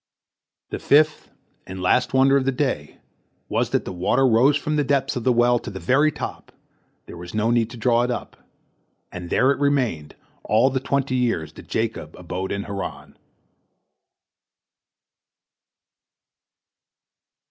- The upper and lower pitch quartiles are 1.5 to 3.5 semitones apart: No, wide, 5.6 semitones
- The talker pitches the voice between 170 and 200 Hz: No, low, 120 Hz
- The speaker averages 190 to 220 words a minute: No, average, 150 wpm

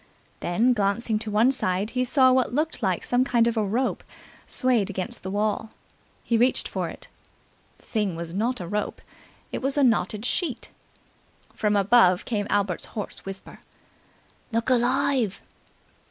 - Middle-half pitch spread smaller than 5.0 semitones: Yes, average, 4.0 semitones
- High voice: Yes, high, 225 Hz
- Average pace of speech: Yes, average, 155 wpm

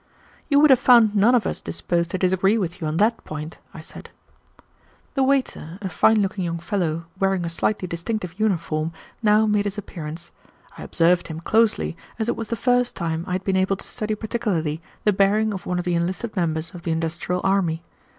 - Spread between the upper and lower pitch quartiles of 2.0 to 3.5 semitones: No, average, 4.2 semitones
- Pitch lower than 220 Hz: Yes, high, 190 Hz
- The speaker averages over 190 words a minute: Yes, fast, 205 wpm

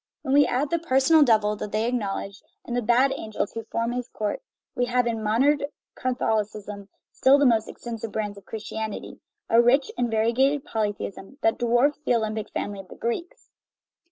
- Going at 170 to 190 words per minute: Yes, average, 180 wpm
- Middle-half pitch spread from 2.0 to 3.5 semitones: Yes, average, 3.2 semitones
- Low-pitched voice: No, high, 230 Hz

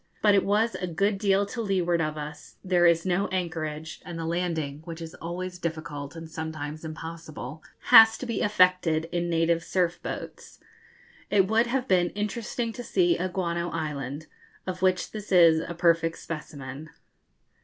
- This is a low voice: No, medium, 170 Hz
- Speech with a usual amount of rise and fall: Yes, average, 3.0 semitones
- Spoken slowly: No, average, 165 wpm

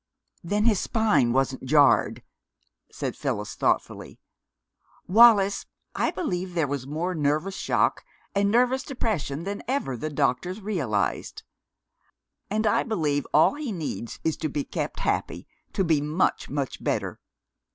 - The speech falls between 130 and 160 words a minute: Yes, slow, 135 wpm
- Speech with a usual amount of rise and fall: No, wide, 6.5 semitones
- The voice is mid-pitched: Yes, medium, 175 Hz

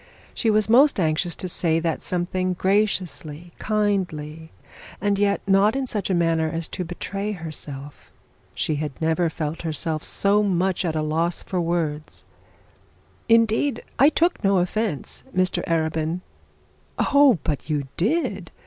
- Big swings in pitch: No, average, 4.3 semitones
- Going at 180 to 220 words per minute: No, average, 140 wpm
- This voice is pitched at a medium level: Yes, medium, 175 Hz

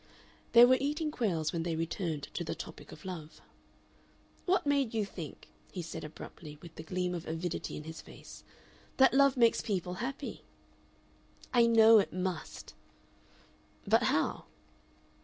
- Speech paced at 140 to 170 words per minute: Yes, average, 150 wpm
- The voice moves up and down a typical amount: No, wide, 6.7 semitones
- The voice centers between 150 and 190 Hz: Yes, medium, 185 Hz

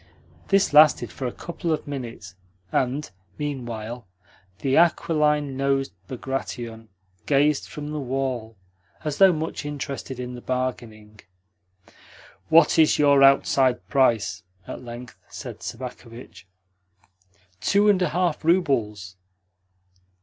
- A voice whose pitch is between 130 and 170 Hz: Yes, low, 135 Hz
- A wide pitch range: No, average, 3.9 semitones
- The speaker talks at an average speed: No, slow, 115 wpm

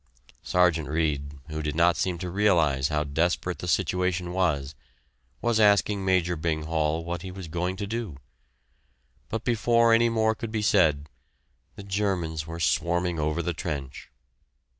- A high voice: No, very low, 85 Hz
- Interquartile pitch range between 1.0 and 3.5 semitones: No, average, 3.9 semitones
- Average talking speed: Yes, average, 155 wpm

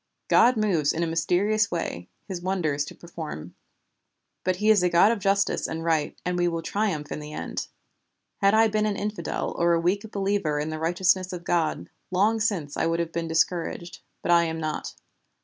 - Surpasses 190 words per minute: Yes, average, 200 wpm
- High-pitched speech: No, medium, 175 Hz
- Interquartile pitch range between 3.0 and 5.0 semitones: Yes, average, 3.6 semitones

